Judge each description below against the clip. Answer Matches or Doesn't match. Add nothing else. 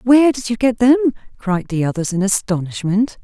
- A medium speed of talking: Matches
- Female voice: Matches